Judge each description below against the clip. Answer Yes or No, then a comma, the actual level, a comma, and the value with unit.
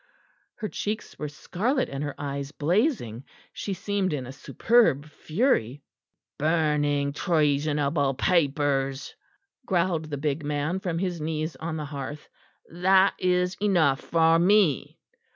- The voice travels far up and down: No, average, 4.1 semitones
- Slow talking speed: Yes, slow, 125 wpm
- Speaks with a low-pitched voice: No, medium, 155 Hz